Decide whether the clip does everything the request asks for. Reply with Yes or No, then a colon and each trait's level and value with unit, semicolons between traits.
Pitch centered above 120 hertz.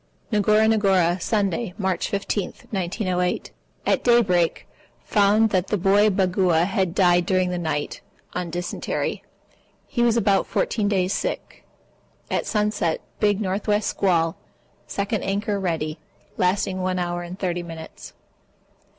Yes: high, 190 Hz